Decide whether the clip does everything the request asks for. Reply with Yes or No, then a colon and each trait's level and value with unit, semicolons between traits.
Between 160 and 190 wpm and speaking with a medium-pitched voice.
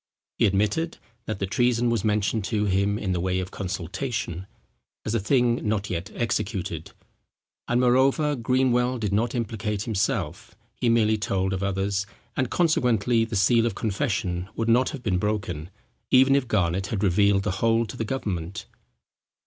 No: average, 165 wpm; low, 105 Hz